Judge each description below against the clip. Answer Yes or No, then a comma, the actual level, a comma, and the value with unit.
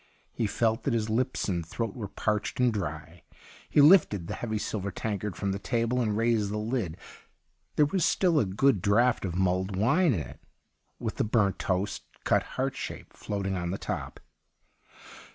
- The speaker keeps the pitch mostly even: No, average, 3.7 semitones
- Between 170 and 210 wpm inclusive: Yes, average, 180 wpm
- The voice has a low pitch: Yes, low, 105 Hz